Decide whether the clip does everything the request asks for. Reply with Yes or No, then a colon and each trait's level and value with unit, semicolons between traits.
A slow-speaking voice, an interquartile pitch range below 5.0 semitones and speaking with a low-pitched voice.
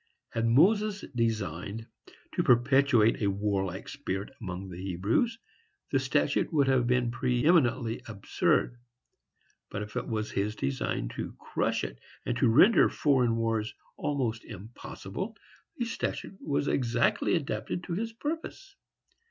No: slow, 130 wpm; wide, 5.4 semitones; low, 120 Hz